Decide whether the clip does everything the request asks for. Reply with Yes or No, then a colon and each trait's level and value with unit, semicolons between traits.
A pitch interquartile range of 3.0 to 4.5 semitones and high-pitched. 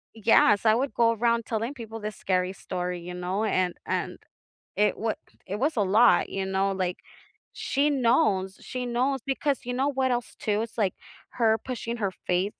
Yes: average, 4.2 semitones; high, 220 Hz